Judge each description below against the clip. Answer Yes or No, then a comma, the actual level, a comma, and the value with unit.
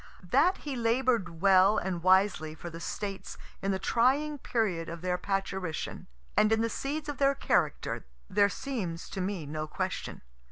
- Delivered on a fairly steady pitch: No, wide, 5.4 semitones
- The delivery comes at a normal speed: Yes, average, 165 wpm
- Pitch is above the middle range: Yes, high, 195 Hz